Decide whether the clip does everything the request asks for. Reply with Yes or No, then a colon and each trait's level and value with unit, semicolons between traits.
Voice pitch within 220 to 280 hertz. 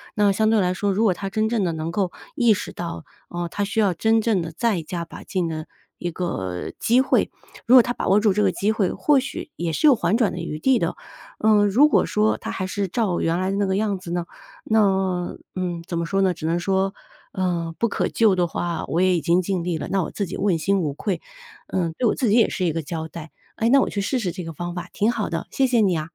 No: high, 190 Hz